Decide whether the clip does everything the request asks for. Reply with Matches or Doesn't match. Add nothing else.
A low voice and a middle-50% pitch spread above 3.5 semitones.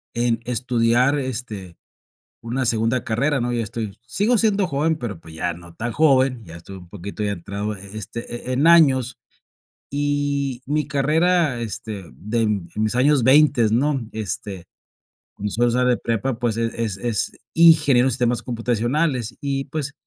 Matches